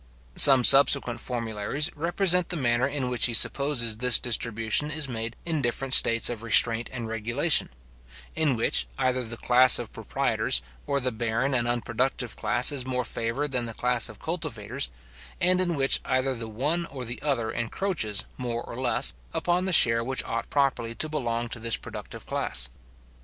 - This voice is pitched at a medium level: No, low, 125 Hz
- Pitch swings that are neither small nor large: Yes, average, 3.4 semitones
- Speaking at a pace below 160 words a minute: No, average, 175 wpm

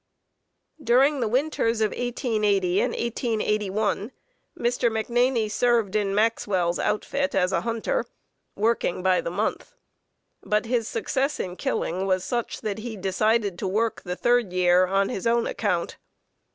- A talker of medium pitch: No, high, 215 Hz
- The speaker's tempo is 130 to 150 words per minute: Yes, average, 145 wpm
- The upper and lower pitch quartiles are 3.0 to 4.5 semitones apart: Yes, average, 3.6 semitones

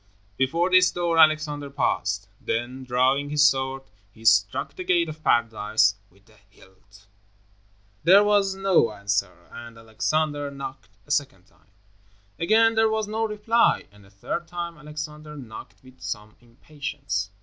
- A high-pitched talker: No, medium, 140 Hz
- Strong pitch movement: Yes, wide, 7.4 semitones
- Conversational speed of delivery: Yes, average, 145 wpm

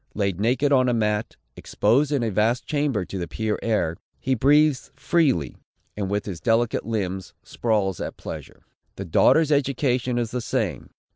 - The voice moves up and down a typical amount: Yes, average, 4.6 semitones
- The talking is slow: No, average, 165 wpm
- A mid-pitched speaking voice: No, low, 115 Hz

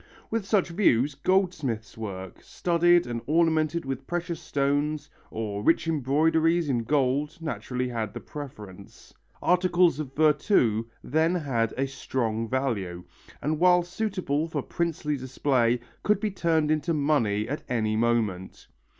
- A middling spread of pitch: No, wide, 6.0 semitones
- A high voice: No, medium, 145 Hz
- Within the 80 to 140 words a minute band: Yes, slow, 135 wpm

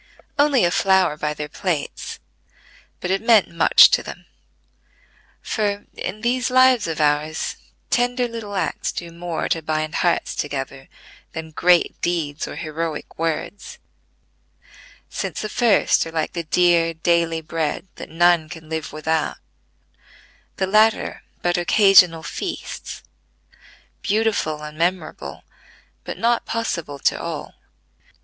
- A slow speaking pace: Yes, slow, 130 wpm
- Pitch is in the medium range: Yes, medium, 170 Hz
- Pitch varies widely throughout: No, average, 4.4 semitones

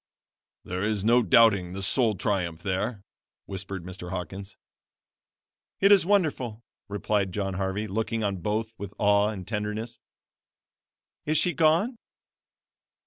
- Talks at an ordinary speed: No, slow, 125 wpm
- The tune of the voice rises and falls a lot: No, average, 3.3 semitones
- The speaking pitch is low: Yes, low, 105 Hz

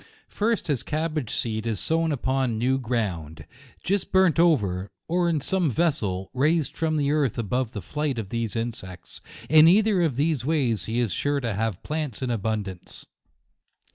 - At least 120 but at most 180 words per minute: Yes, average, 170 wpm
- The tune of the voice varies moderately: No, wide, 6.2 semitones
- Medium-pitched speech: No, low, 130 Hz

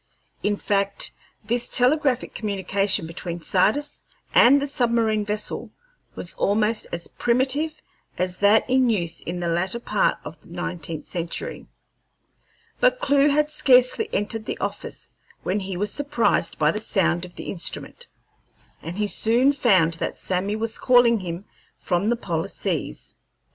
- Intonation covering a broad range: Yes, wide, 5.7 semitones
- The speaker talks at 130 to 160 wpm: Yes, average, 150 wpm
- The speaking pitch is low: No, high, 210 Hz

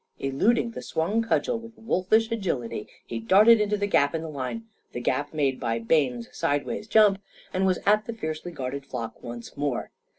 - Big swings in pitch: Yes, wide, 8.1 semitones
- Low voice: No, medium, 160 Hz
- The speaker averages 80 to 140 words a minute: No, average, 185 wpm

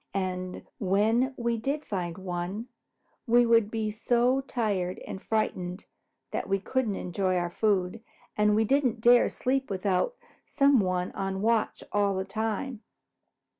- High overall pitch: Yes, high, 210 Hz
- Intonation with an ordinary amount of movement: Yes, average, 3.9 semitones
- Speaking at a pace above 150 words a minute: No, average, 145 wpm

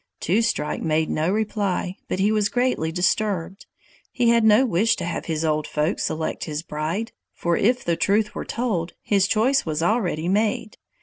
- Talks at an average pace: Yes, average, 180 wpm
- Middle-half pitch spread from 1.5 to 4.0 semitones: No, average, 5.1 semitones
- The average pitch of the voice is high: Yes, high, 195 Hz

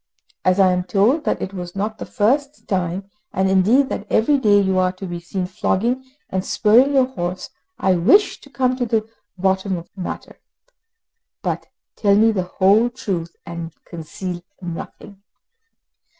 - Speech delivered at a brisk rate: No, average, 165 wpm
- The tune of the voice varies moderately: Yes, average, 3.8 semitones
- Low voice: No, high, 195 Hz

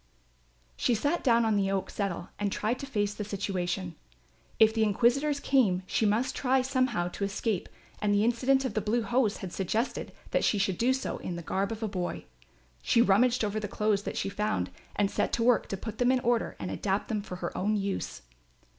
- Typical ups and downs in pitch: Yes, average, 3.6 semitones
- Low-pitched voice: No, high, 215 Hz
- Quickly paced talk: Yes, fast, 215 wpm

